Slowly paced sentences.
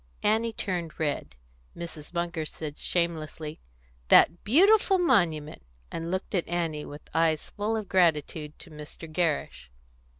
Yes: slow, 130 wpm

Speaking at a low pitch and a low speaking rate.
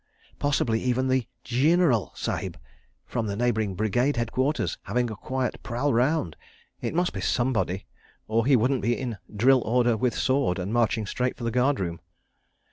No: low, 120 Hz; average, 165 wpm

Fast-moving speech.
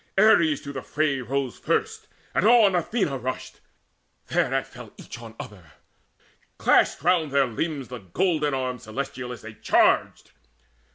No: average, 140 wpm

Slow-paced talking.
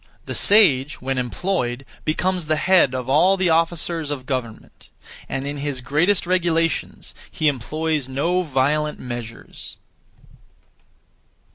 Yes: slow, 120 wpm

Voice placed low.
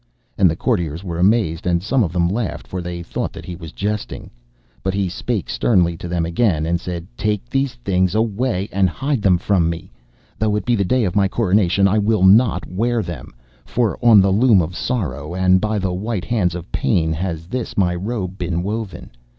Yes: very low, 95 Hz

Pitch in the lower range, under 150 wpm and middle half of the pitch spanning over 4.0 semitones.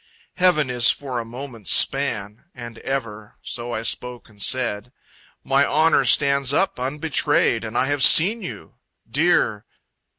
No: low, 130 Hz; average, 140 wpm; average, 3.5 semitones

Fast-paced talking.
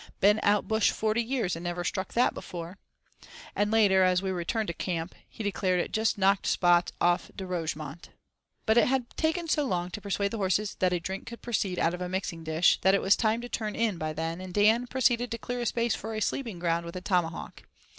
Yes: fast, 230 wpm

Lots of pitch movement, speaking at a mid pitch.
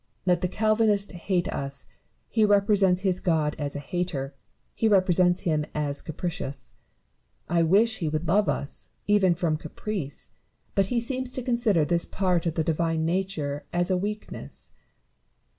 No: average, 4.2 semitones; medium, 180 Hz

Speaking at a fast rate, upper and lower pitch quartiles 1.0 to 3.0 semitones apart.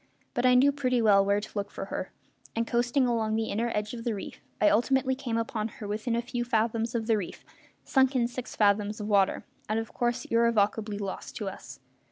Yes: fast, 220 wpm; narrow, 2.5 semitones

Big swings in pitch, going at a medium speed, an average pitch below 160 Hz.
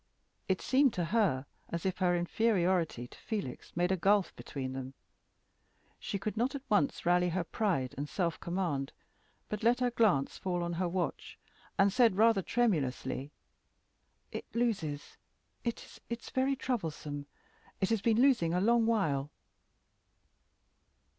No: wide, 5.7 semitones; average, 145 wpm; medium, 185 Hz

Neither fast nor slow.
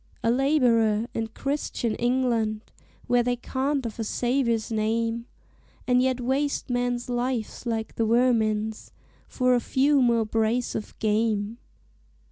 No: slow, 130 wpm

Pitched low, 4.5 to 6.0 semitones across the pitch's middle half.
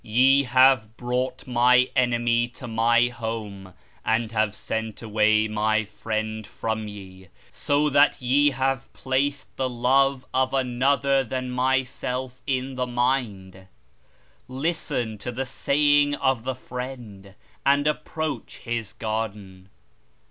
No: low, 125 Hz; average, 3.3 semitones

